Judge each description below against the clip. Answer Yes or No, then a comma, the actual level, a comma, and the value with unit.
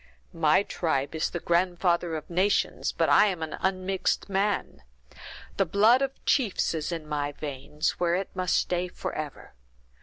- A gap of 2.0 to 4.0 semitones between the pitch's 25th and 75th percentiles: Yes, average, 3.5 semitones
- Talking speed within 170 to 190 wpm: No, average, 155 wpm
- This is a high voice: No, medium, 175 Hz